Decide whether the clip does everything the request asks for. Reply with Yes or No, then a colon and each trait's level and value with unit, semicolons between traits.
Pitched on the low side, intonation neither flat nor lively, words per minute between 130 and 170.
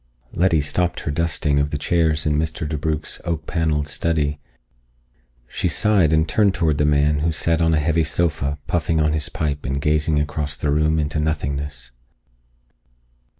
No: very low, 75 Hz; narrow, 1.8 semitones; average, 165 wpm